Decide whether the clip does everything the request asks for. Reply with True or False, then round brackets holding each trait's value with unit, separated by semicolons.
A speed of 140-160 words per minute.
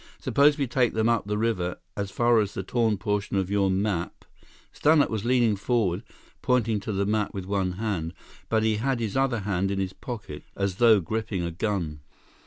False (195 wpm)